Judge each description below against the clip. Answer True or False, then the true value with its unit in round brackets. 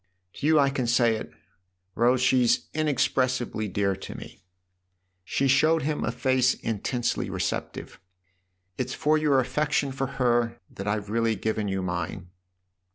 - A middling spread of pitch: True (4.7 semitones)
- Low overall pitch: True (120 Hz)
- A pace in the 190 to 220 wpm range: False (160 wpm)